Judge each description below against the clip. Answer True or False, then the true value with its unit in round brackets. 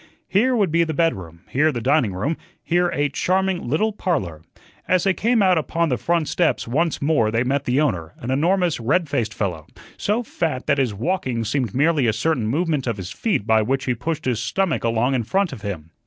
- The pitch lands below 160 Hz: True (140 Hz)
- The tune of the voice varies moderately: False (7.0 semitones)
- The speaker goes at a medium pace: False (215 wpm)